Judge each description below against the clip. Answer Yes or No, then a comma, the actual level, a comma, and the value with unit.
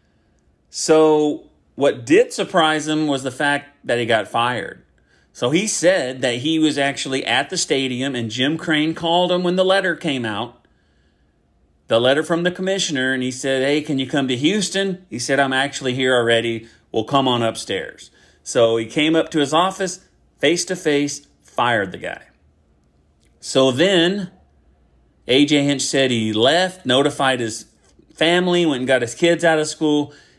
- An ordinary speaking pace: Yes, average, 170 wpm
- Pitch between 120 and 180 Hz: Yes, medium, 140 Hz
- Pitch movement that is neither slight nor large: No, wide, 5.8 semitones